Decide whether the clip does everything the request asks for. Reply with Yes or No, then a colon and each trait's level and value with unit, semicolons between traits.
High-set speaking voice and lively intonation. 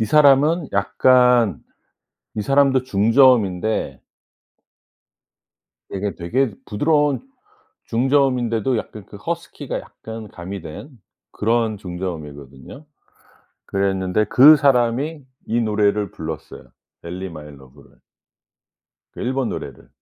No: low, 110 Hz; wide, 5.8 semitones